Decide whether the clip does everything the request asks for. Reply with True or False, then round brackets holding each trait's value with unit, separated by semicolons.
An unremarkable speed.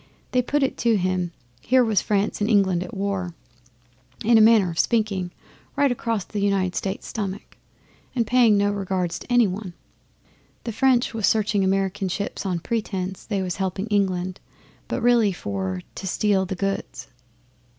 True (165 wpm)